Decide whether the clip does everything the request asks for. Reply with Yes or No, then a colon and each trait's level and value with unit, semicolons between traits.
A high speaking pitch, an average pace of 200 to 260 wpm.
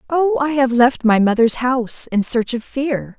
Yes: very high, 255 Hz; fast, 205 wpm